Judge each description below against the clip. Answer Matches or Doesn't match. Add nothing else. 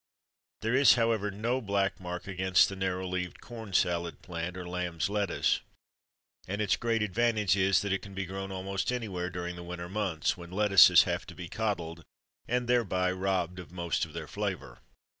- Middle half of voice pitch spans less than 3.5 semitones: Matches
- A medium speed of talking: Matches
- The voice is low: Matches